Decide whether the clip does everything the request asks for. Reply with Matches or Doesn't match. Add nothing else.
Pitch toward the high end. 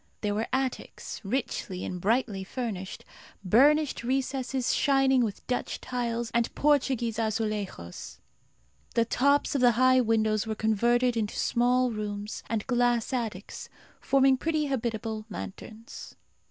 Matches